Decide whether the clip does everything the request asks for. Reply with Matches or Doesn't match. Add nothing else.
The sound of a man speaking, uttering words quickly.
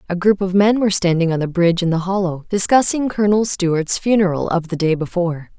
Doesn't match